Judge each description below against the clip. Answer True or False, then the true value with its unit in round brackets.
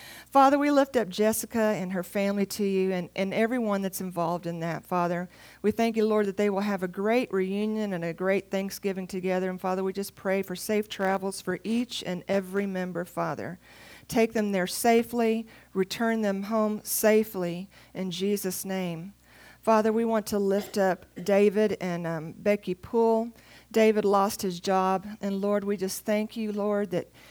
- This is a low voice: False (200 Hz)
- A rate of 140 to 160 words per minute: False (180 wpm)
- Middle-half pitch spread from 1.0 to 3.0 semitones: True (2.5 semitones)